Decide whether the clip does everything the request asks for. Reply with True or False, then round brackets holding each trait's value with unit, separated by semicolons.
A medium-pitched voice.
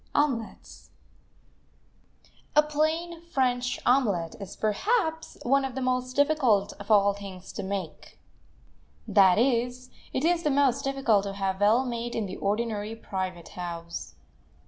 False (235 Hz)